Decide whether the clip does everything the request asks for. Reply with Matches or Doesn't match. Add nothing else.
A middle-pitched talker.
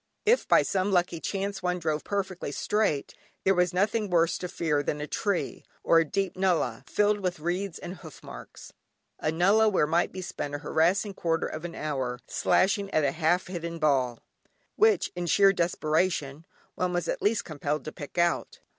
Matches